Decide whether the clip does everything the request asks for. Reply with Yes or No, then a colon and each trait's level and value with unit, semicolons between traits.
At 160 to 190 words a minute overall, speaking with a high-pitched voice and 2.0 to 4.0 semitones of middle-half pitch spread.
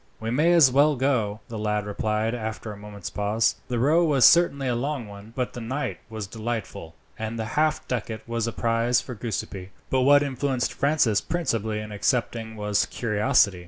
No: average, 185 wpm; low, 115 Hz; average, 3.7 semitones